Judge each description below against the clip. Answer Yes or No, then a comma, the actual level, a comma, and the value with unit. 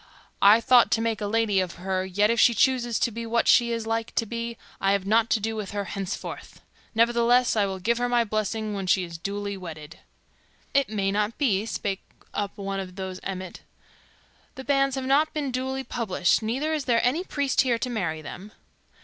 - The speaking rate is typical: No, fast, 215 wpm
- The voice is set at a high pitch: Yes, high, 220 Hz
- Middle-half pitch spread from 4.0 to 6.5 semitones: No, average, 3.6 semitones